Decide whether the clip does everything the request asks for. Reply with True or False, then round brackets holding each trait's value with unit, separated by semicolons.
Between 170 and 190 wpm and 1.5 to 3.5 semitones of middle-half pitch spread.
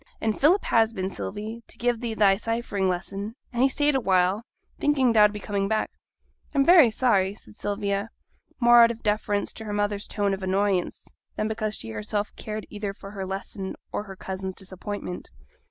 True (185 wpm; 2.6 semitones)